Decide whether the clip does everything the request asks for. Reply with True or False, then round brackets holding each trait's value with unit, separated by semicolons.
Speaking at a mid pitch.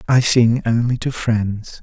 False (115 Hz)